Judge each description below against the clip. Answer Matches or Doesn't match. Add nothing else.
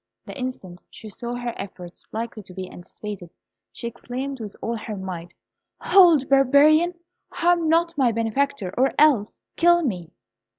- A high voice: Matches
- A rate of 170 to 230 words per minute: Doesn't match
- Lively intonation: Matches